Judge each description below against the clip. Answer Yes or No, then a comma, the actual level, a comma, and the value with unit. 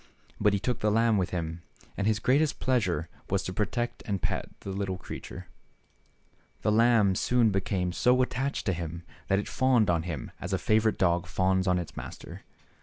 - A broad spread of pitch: No, average, 4.0 semitones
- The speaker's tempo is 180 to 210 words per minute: Yes, average, 190 wpm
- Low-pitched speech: Yes, low, 100 Hz